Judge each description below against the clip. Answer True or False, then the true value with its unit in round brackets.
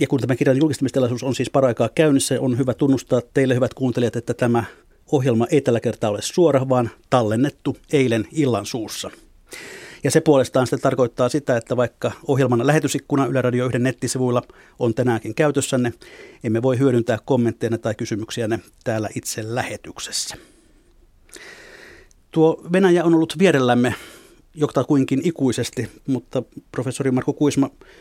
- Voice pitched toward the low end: True (130 Hz)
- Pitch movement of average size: True (3.1 semitones)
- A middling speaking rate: True (140 wpm)